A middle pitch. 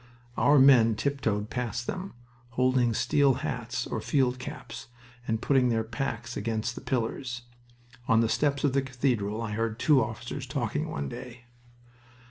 No: low, 125 Hz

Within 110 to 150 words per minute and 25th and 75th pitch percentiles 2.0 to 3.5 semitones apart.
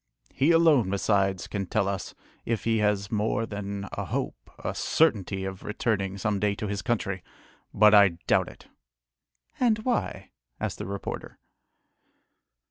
Yes: average, 145 wpm; narrow, 2.4 semitones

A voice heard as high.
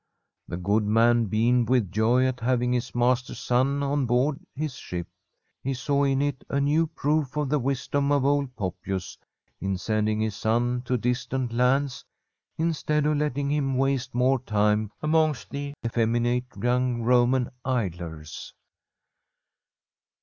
No: low, 125 Hz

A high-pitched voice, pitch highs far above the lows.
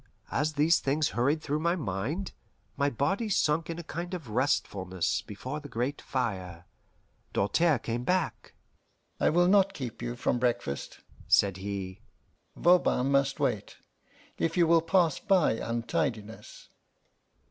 No: medium, 140 Hz; wide, 6.3 semitones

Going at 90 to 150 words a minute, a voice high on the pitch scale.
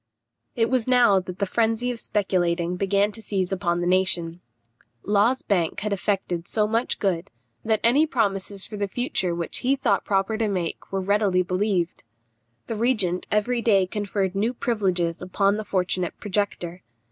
No: average, 165 wpm; high, 200 Hz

